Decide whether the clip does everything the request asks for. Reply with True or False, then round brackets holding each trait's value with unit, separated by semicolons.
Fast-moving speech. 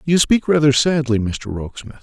False (175 wpm)